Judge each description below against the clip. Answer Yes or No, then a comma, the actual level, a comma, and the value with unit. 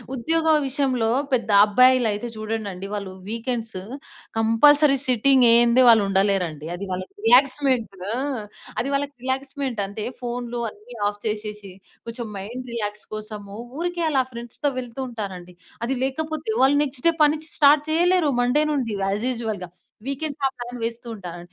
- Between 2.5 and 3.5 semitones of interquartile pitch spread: No, average, 4.5 semitones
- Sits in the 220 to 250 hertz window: Yes, high, 235 Hz